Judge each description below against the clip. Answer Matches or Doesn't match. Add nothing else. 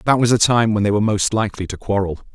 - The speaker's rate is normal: Doesn't match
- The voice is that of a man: Matches